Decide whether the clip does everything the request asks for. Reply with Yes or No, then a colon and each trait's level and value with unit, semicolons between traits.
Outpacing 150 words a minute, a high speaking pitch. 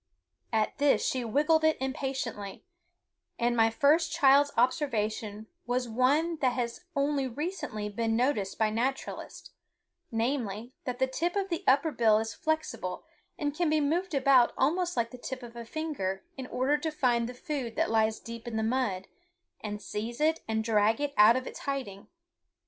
Yes: average, 170 wpm; very high, 255 Hz